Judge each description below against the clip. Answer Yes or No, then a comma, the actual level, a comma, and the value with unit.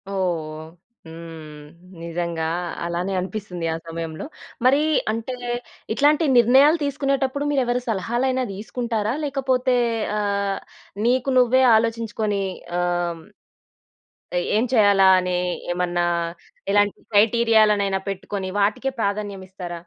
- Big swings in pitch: Yes, wide, 5.7 semitones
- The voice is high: Yes, high, 205 Hz